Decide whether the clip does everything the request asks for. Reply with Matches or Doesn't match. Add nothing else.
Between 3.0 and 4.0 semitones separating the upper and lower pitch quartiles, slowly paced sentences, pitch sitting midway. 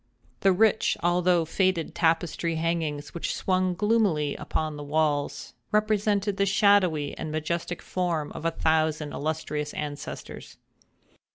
Matches